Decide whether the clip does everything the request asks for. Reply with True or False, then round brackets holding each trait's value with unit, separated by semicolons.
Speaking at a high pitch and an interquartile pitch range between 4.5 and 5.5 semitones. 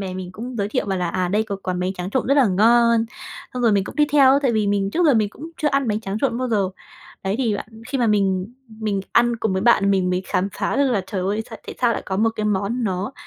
False (210 Hz; 3.8 semitones)